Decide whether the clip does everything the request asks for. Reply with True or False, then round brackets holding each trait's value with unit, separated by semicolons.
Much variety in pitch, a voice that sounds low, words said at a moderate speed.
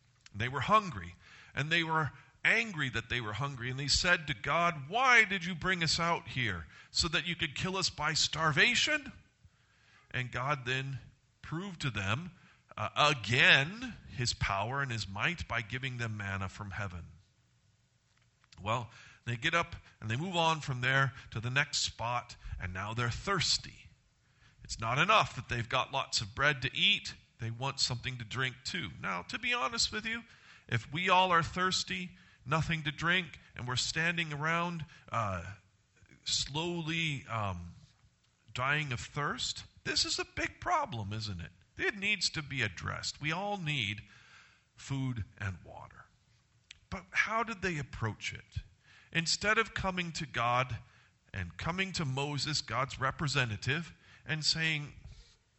True (6.2 semitones; 130 Hz; 160 wpm)